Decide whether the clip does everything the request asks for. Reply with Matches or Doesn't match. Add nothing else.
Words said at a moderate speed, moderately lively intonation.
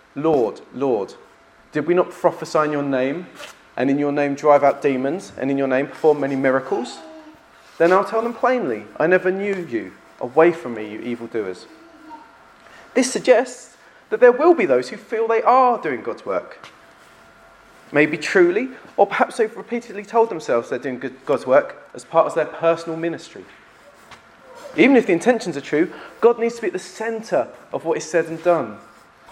Doesn't match